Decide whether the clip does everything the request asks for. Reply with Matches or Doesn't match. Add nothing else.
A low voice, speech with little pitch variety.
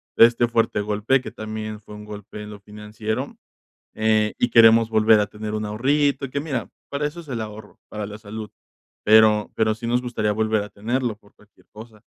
Matches